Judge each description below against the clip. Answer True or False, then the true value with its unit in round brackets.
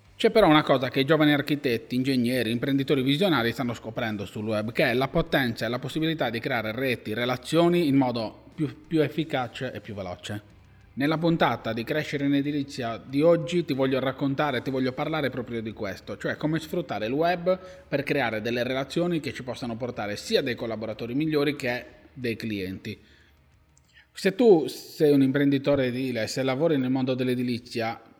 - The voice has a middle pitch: False (130 Hz)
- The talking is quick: True (175 wpm)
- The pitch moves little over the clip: False (4.4 semitones)